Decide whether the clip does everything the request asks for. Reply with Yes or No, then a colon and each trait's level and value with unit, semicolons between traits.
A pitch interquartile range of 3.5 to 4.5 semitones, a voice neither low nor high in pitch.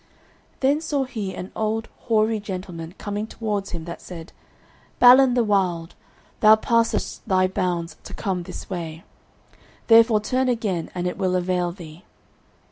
No: average, 4.1 semitones; high, 200 Hz